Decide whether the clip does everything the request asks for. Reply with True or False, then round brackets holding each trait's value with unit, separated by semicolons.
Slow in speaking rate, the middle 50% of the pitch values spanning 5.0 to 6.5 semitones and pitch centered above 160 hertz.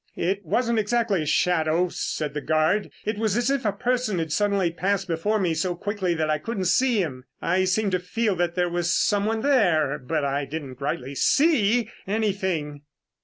False (185 wpm; 5.3 semitones; 185 Hz)